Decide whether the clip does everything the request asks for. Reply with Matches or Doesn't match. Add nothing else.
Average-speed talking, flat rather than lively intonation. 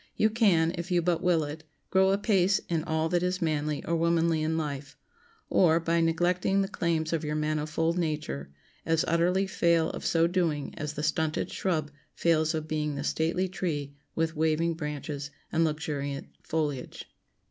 Matches